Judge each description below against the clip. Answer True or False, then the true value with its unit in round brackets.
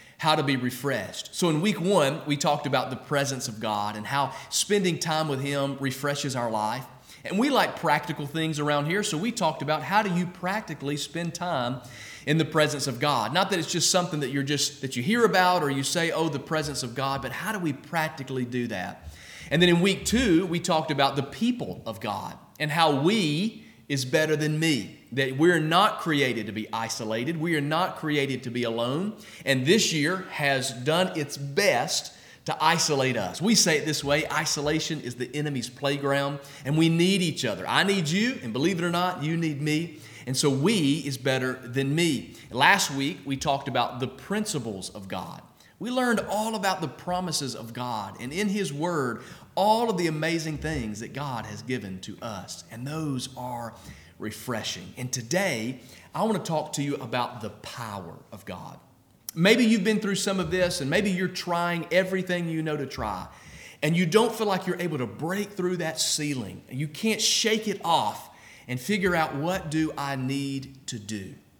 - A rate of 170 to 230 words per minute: True (200 wpm)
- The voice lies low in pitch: False (150 Hz)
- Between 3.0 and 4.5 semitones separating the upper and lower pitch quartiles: False (5.0 semitones)